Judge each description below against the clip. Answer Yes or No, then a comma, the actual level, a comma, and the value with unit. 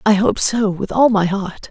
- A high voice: Yes, high, 205 Hz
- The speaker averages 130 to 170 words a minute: No, fast, 245 wpm